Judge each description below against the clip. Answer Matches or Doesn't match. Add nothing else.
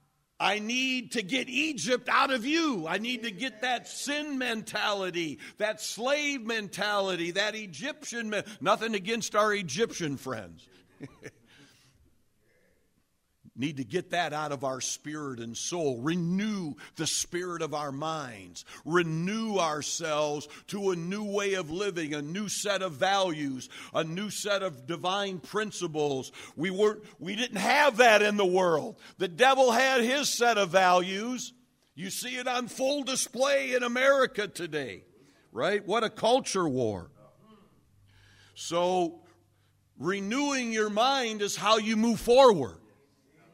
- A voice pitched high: Matches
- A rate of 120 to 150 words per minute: Matches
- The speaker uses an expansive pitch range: Matches